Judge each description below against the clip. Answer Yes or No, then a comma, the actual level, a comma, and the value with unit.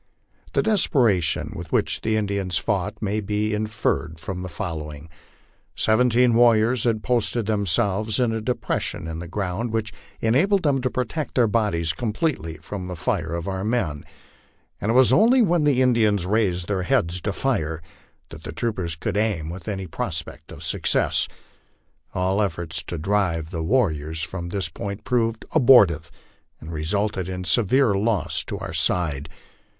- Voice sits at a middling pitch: No, low, 100 Hz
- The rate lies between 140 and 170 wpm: Yes, average, 160 wpm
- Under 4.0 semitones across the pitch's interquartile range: No, average, 5.1 semitones